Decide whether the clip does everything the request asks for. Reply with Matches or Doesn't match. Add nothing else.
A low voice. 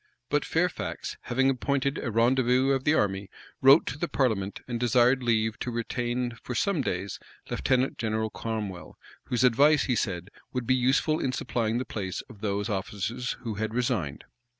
Matches